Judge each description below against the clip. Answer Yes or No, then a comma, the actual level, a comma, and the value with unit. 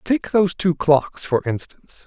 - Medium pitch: Yes, medium, 170 Hz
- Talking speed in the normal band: Yes, average, 175 wpm